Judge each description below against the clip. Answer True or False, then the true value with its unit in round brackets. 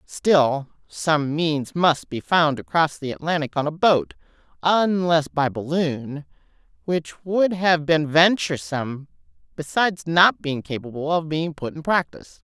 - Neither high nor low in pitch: True (160 Hz)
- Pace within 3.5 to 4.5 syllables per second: True (4.2 syllables/s)